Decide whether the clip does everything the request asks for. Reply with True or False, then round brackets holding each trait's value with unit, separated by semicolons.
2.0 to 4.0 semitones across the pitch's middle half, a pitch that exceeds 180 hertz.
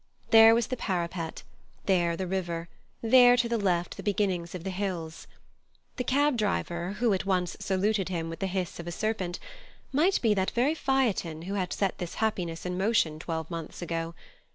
False (4.4 semitones; 190 Hz)